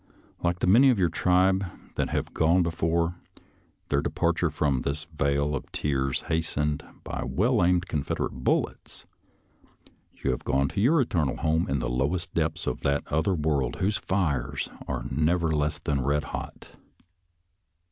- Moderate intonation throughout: Yes, average, 3.8 semitones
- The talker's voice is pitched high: No, very low, 80 Hz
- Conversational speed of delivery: Yes, average, 155 wpm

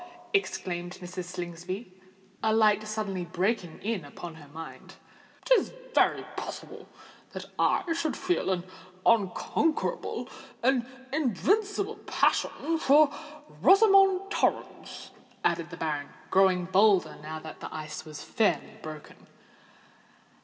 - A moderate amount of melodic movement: No, wide, 8.7 semitones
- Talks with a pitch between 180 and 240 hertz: Yes, high, 190 Hz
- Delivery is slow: Yes, slow, 110 wpm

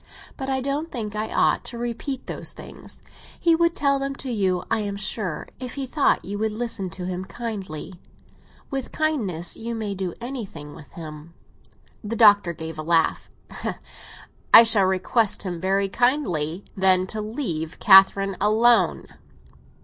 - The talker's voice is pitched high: Yes, high, 210 Hz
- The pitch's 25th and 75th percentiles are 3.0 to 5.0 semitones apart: Yes, average, 4.7 semitones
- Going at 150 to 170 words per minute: Yes, average, 155 wpm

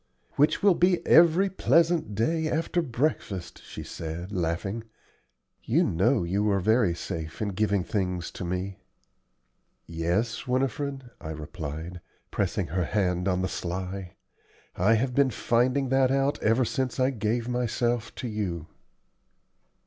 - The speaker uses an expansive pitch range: Yes, wide, 6.5 semitones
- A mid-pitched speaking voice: No, low, 110 Hz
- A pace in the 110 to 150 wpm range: Yes, slow, 135 wpm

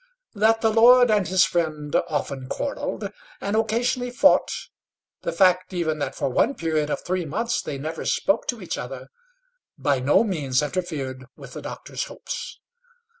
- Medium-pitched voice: Yes, medium, 175 Hz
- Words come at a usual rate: Yes, average, 160 wpm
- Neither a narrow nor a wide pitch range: No, wide, 7.0 semitones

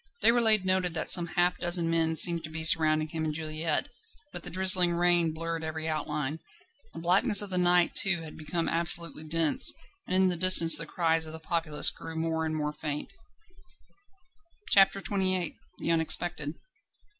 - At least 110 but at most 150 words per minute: No, average, 170 wpm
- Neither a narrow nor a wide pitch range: No, narrow, 2.1 semitones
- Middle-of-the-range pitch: Yes, medium, 165 Hz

